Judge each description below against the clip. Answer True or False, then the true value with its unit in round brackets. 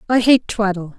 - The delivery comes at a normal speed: True (180 wpm)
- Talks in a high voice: True (215 Hz)